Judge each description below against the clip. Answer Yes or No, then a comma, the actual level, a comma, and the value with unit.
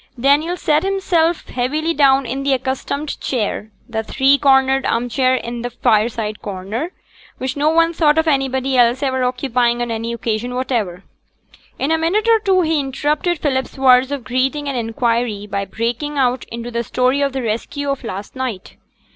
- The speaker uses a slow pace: No, average, 175 wpm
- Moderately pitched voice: No, very high, 260 Hz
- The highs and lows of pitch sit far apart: No, average, 3.5 semitones